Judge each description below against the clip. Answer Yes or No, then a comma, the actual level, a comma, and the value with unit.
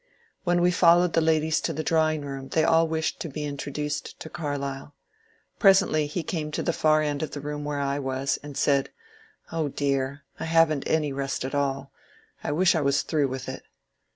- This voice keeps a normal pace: No, fast, 210 wpm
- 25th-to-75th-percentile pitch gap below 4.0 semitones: Yes, narrow, 2.4 semitones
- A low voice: No, medium, 150 Hz